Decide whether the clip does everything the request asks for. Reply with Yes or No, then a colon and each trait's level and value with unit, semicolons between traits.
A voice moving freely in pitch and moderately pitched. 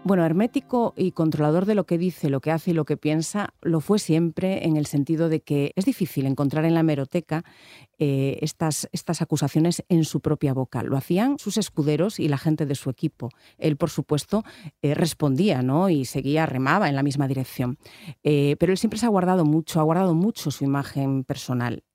No: average, 3.6 semitones; medium, 155 Hz